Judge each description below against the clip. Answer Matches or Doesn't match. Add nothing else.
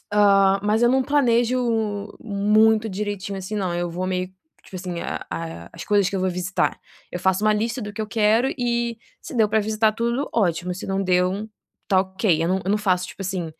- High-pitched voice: Matches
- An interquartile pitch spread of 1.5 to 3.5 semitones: Matches